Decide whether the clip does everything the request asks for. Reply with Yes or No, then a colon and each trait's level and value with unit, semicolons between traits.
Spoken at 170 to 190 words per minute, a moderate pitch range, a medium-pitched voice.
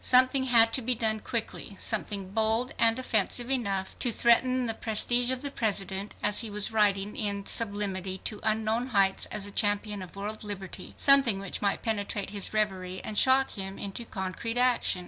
No: average, 180 wpm; average, 3.0 semitones; high, 215 Hz